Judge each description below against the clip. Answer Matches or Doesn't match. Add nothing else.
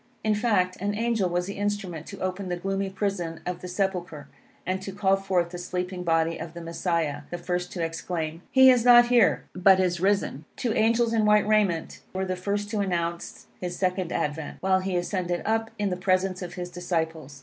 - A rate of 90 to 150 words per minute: Doesn't match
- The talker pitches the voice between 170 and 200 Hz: Matches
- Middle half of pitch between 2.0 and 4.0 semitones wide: Matches